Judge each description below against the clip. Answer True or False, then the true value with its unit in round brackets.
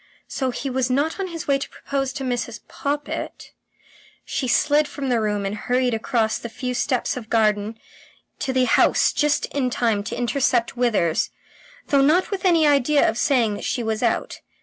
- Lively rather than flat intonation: False (3.6 semitones)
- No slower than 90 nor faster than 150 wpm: False (185 wpm)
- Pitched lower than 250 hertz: False (255 Hz)